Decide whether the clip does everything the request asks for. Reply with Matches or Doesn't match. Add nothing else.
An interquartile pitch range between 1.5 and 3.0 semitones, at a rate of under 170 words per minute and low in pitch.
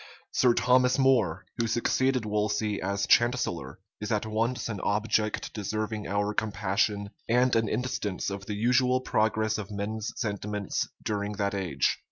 Matches